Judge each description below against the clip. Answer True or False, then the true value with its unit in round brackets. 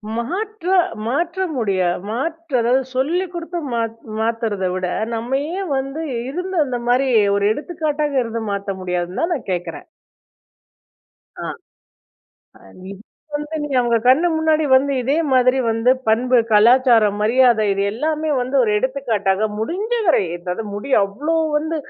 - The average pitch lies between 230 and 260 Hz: True (255 Hz)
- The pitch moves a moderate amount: False (6.1 semitones)